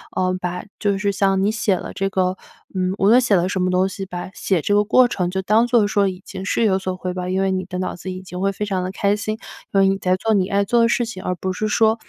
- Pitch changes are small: Yes, narrow, 2.0 semitones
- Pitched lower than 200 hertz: Yes, high, 190 Hz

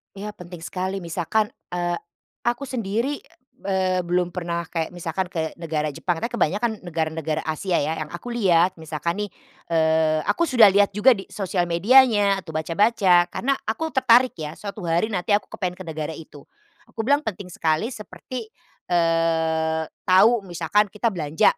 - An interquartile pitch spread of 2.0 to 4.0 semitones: No, average, 4.4 semitones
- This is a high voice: No, medium, 180 Hz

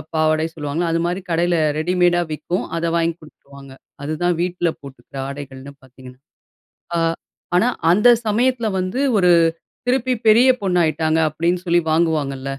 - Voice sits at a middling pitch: Yes, medium, 165 Hz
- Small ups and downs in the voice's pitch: No, average, 3.5 semitones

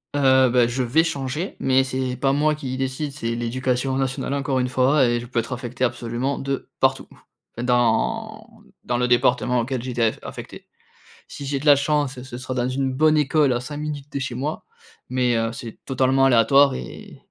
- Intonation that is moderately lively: No, narrow, 2.3 semitones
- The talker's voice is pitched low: Yes, low, 130 Hz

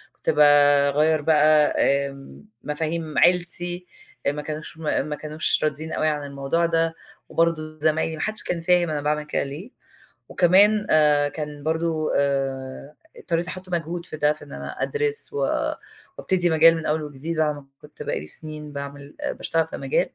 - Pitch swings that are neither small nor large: No, narrow, 2.3 semitones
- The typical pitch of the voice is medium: Yes, medium, 155 Hz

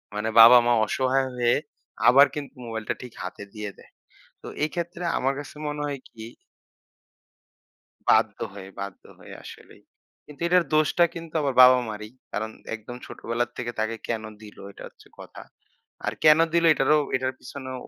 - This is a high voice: No, low, 125 Hz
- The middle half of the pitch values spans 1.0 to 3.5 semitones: No, average, 4.5 semitones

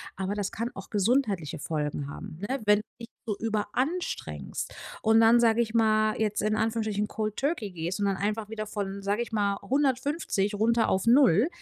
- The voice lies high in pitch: Yes, high, 215 Hz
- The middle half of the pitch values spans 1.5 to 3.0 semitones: Yes, narrow, 2.5 semitones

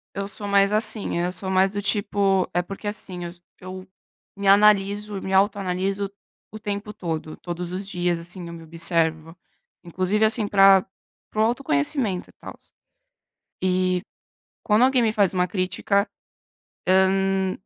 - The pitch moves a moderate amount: No, narrow, 2.2 semitones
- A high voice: Yes, high, 195 Hz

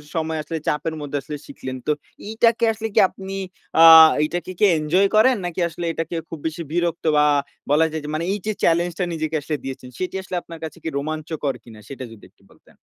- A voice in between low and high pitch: Yes, medium, 160 Hz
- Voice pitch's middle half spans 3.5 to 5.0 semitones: No, average, 2.8 semitones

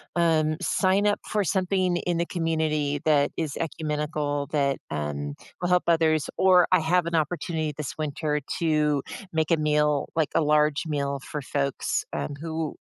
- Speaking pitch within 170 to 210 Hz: No, medium, 155 Hz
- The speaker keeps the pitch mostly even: Yes, narrow, 2.3 semitones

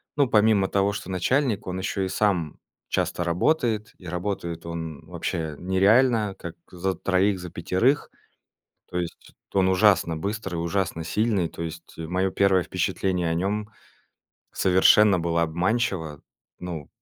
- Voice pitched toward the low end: Yes, very low, 95 Hz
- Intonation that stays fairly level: No, average, 3.3 semitones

